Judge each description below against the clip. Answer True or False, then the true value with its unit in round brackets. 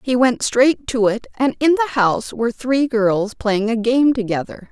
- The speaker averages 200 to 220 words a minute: True (205 wpm)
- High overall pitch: True (240 Hz)